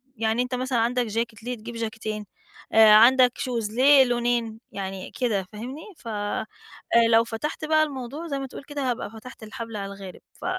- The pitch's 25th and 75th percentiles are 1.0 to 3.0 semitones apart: Yes, average, 2.7 semitones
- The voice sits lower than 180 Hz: No, high, 235 Hz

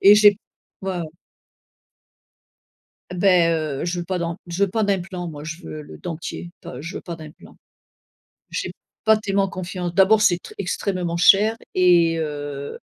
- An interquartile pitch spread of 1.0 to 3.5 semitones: Yes, average, 2.9 semitones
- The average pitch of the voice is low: No, medium, 175 Hz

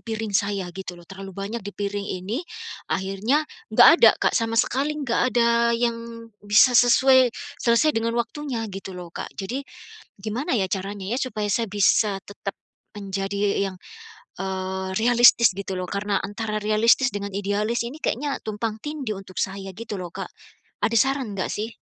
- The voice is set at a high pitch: Yes, high, 210 Hz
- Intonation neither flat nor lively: Yes, average, 3.2 semitones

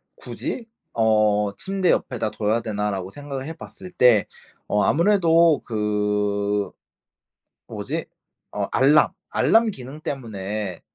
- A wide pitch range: Yes, wide, 6.9 semitones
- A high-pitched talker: No, low, 110 Hz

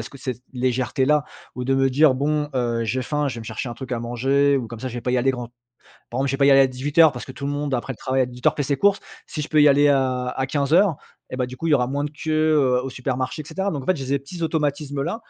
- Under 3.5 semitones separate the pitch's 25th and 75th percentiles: Yes, narrow, 2.5 semitones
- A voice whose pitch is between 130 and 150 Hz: Yes, low, 135 Hz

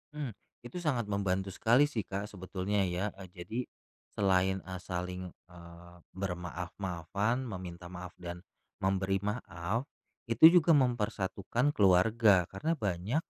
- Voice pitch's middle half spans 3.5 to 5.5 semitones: Yes, average, 4.1 semitones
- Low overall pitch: Yes, very low, 95 Hz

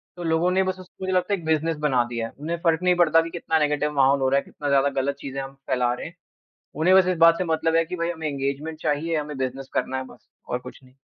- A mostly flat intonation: No, average, 3.6 semitones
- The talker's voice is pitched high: No, medium, 155 Hz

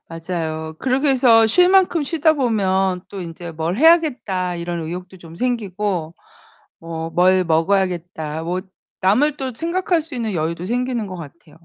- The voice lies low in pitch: No, high, 190 Hz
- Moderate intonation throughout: No, wide, 7.0 semitones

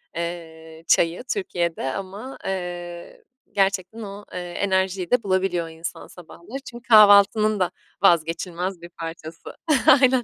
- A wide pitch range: No, average, 3.0 semitones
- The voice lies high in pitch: No, medium, 180 Hz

